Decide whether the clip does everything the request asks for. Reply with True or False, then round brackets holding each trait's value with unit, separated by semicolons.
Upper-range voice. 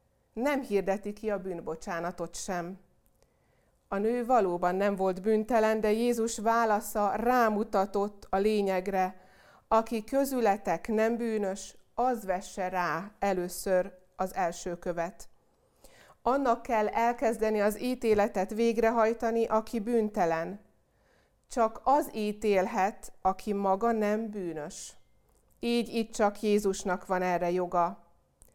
True (205 Hz)